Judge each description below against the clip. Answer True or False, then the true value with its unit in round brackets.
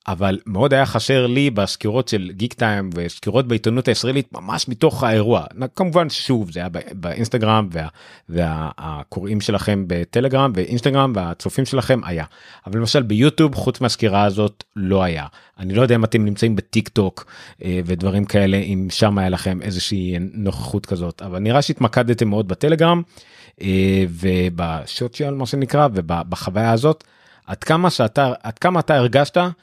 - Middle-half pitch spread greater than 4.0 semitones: True (5.6 semitones)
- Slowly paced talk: False (140 wpm)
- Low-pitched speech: True (110 Hz)